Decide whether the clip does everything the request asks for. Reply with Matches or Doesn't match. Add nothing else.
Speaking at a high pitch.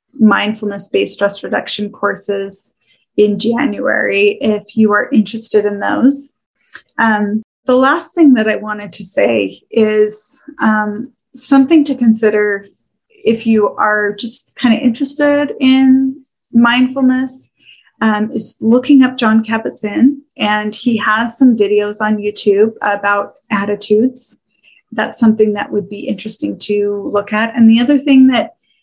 Matches